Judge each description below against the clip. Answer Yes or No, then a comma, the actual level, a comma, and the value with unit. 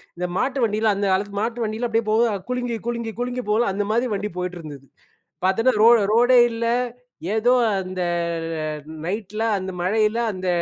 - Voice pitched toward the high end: Yes, high, 220 Hz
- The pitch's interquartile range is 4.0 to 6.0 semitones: No, average, 3.5 semitones